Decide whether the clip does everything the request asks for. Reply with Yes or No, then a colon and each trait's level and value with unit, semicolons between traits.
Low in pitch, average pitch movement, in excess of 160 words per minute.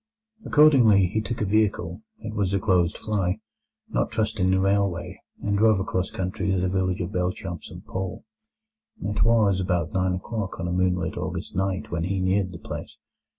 No: very low, 95 Hz; narrow, 2.3 semitones; average, 170 wpm